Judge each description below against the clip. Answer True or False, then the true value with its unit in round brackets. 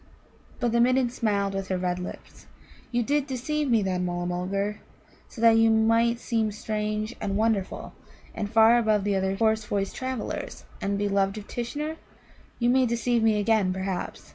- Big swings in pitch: False (3.1 semitones)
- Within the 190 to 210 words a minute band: False (170 wpm)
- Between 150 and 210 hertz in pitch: False (220 Hz)